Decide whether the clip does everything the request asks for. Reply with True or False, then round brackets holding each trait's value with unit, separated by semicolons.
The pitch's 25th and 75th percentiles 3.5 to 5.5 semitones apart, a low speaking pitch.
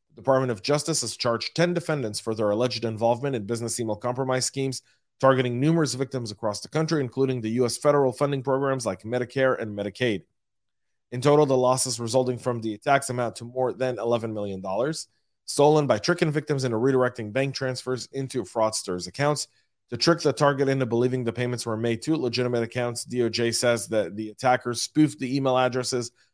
False (2.7 semitones; 125 Hz)